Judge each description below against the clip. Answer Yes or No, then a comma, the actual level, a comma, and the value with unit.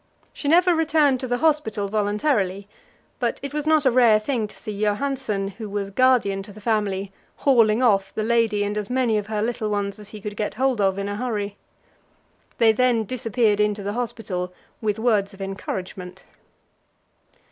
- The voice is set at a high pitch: Yes, high, 215 Hz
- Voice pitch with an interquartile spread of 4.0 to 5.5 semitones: No, average, 3.6 semitones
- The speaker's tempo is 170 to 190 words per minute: Yes, average, 180 wpm